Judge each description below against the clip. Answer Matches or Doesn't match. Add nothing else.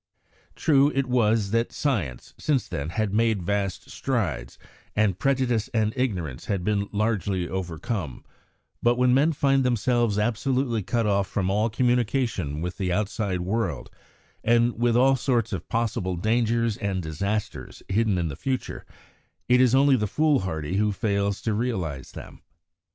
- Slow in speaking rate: Doesn't match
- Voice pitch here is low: Matches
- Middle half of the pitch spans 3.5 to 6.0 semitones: Matches